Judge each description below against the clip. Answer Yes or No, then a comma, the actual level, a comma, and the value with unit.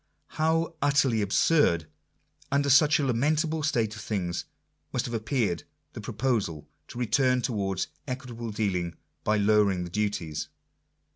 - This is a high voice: No, low, 115 Hz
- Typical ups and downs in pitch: No, wide, 5.8 semitones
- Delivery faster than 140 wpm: No, slow, 135 wpm